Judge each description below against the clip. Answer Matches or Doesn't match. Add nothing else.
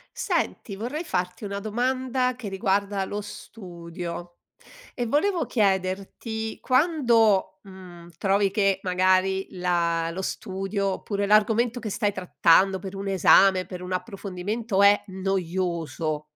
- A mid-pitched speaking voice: Doesn't match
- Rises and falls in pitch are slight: Doesn't match